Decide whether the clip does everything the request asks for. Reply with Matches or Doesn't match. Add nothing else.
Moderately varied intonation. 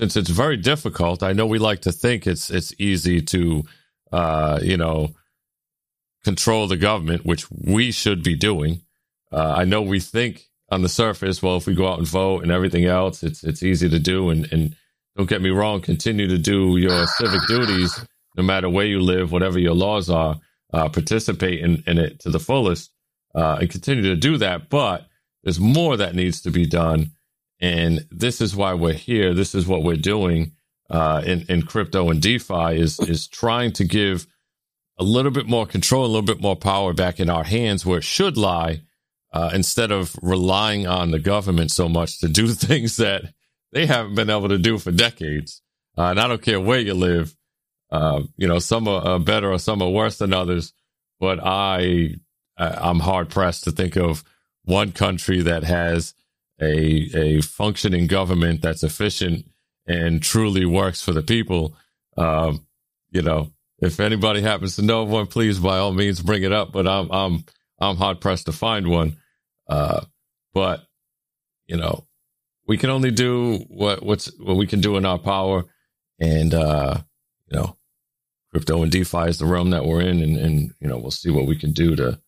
Matches